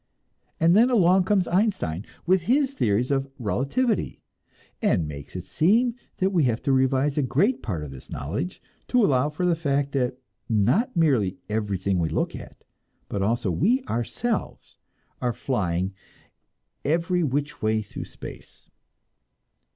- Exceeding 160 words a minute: No, average, 145 wpm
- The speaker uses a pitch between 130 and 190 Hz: Yes, medium, 140 Hz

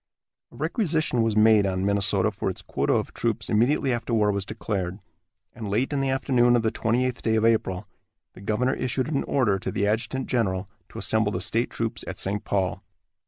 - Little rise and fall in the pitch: No, average, 3.8 semitones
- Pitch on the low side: Yes, low, 110 Hz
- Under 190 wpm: No, fast, 205 wpm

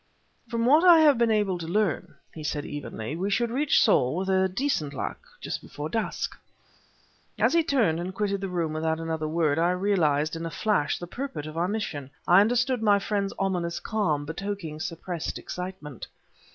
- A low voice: No, medium, 180 Hz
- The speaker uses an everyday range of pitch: Yes, average, 5.0 semitones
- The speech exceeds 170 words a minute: Yes, average, 180 wpm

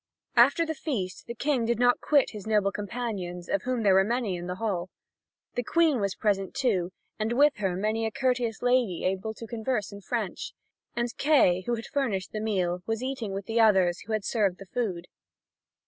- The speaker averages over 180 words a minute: Yes, average, 200 wpm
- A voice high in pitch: Yes, high, 220 Hz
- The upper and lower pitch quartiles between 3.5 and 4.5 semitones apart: Yes, average, 4.2 semitones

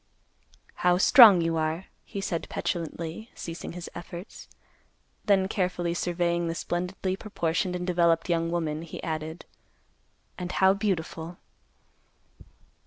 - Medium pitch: Yes, medium, 175 Hz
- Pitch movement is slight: Yes, narrow, 1.9 semitones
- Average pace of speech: No, slow, 115 wpm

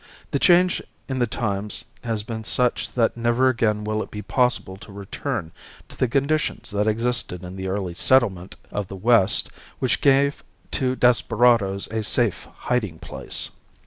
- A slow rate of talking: No, average, 160 wpm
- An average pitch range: Yes, average, 3.6 semitones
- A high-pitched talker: No, low, 115 Hz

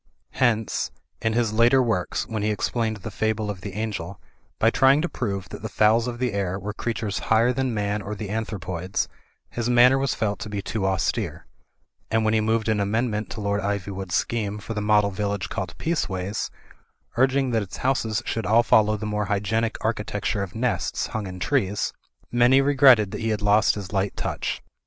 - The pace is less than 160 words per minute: No, average, 195 wpm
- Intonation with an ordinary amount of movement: No, narrow, 2.3 semitones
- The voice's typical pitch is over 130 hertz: No, low, 105 Hz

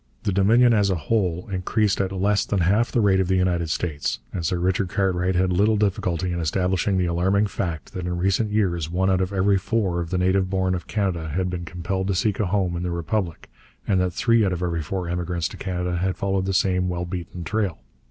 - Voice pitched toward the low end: Yes, very low, 95 Hz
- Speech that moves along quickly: Yes, fast, 230 wpm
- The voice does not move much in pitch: Yes, narrow, 1.9 semitones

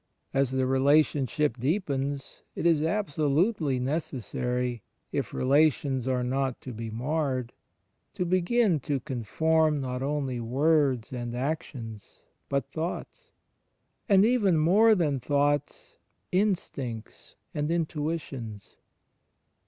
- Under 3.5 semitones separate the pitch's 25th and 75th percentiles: No, average, 4.0 semitones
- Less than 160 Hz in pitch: Yes, medium, 140 Hz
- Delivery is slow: Yes, slow, 105 wpm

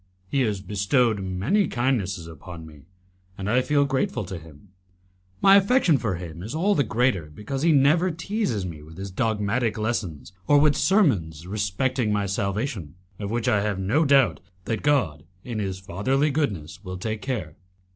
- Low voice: Yes, low, 105 Hz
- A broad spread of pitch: Yes, wide, 6.6 semitones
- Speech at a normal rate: Yes, average, 170 wpm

